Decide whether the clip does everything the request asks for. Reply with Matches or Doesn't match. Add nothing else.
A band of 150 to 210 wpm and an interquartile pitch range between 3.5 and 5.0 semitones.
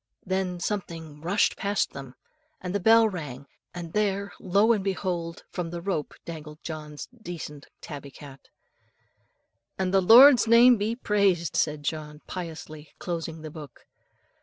Doesn't match